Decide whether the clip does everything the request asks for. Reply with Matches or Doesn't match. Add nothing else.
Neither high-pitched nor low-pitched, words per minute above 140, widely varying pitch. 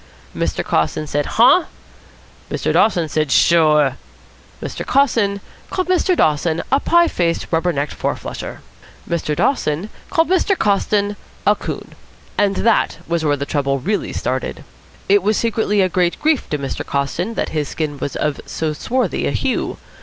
Matches